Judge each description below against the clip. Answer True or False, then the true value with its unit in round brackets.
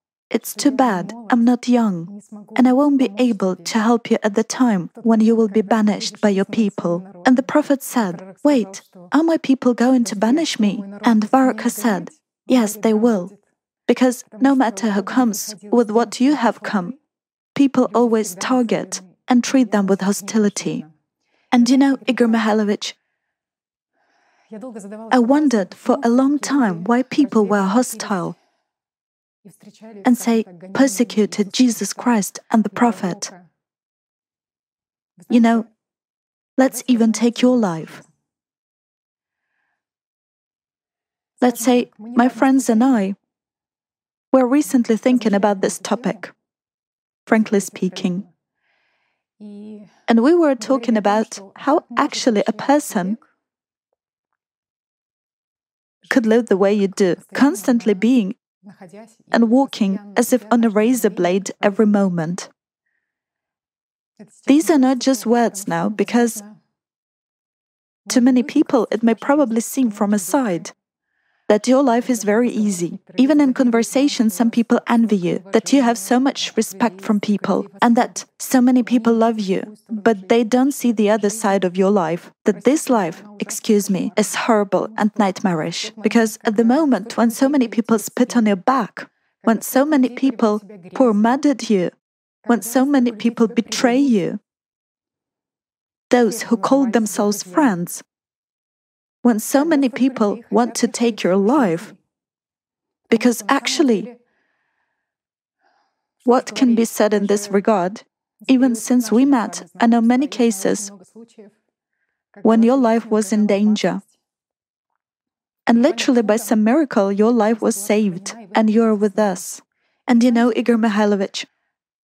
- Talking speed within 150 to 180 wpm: False (135 wpm)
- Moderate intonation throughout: True (3.4 semitones)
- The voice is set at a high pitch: True (230 Hz)